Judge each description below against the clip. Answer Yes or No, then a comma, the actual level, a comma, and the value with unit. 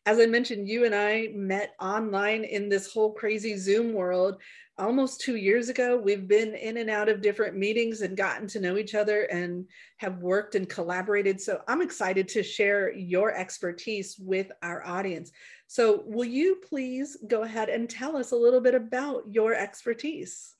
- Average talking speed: Yes, average, 180 wpm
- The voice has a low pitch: No, high, 215 Hz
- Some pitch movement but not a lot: Yes, average, 3.2 semitones